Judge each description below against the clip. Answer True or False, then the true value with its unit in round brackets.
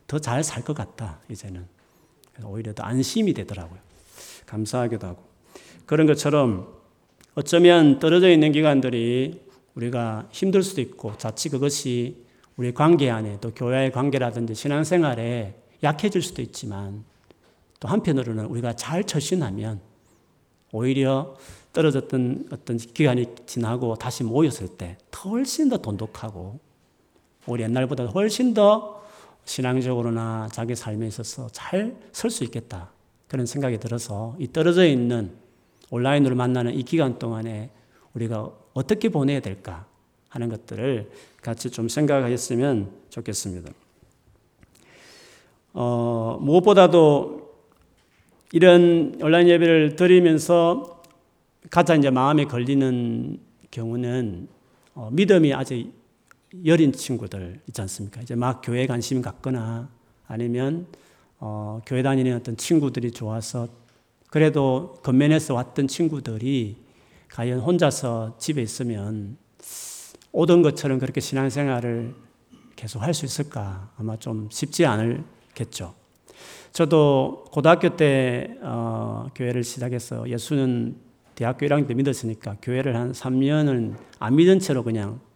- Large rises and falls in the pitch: False (4.5 semitones)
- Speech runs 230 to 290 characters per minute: True (275 characters per minute)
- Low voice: True (125 Hz)